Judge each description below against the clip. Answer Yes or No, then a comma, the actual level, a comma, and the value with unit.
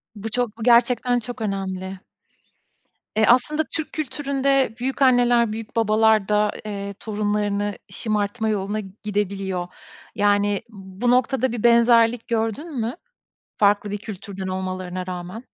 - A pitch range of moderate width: Yes, average, 3.2 semitones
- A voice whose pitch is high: Yes, high, 215 Hz